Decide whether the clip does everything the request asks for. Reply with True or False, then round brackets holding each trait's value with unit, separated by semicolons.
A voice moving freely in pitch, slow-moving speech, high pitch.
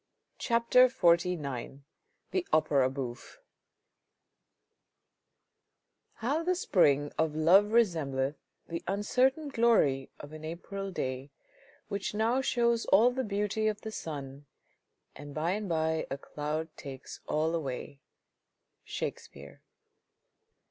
False (7.3 semitones; 110 wpm; 170 Hz)